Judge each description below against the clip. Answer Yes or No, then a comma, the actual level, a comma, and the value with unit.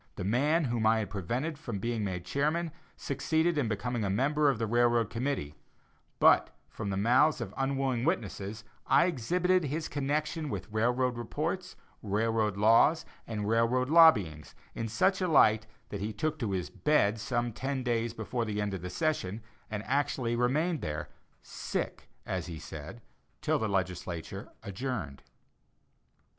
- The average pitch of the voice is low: Yes, low, 120 Hz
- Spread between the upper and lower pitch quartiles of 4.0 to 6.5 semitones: Yes, wide, 5.4 semitones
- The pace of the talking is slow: No, average, 155 wpm